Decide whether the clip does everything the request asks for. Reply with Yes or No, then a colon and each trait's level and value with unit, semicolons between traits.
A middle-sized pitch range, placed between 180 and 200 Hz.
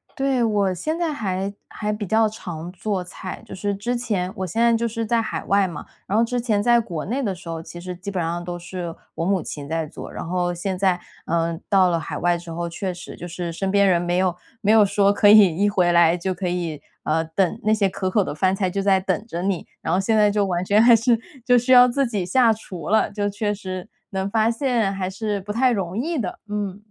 Yes: average, 3.6 semitones; high, 195 Hz